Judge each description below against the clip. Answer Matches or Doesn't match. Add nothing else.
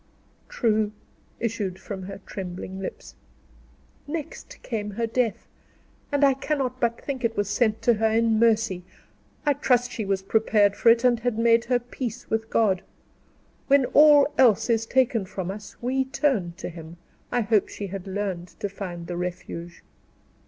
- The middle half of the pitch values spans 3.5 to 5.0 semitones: Matches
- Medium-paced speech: Matches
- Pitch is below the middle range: Doesn't match